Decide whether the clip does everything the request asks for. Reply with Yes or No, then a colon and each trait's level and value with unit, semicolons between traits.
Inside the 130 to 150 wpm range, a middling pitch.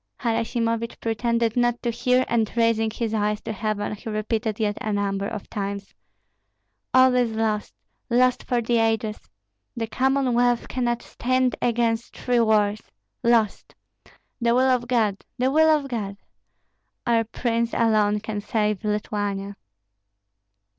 No: slow, 135 wpm; high, 230 Hz